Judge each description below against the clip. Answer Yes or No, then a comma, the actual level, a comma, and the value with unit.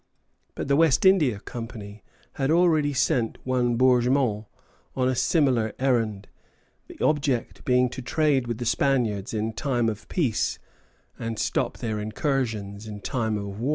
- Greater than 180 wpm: No, average, 150 wpm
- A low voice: Yes, low, 120 Hz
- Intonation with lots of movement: No, average, 3.8 semitones